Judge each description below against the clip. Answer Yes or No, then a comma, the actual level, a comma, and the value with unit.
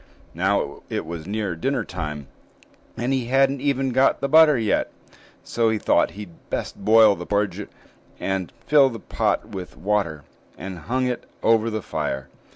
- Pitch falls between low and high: No, low, 110 Hz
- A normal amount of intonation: No, wide, 5.9 semitones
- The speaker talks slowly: No, average, 165 wpm